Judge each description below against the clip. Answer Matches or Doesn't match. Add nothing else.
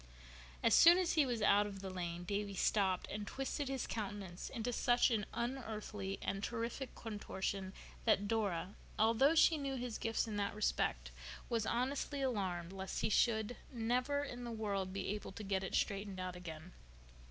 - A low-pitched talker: Doesn't match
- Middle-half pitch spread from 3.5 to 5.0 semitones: Matches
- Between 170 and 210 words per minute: Matches